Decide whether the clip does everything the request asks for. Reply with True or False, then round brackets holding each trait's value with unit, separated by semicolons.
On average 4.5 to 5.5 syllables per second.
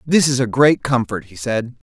True (4.8 syllables/s)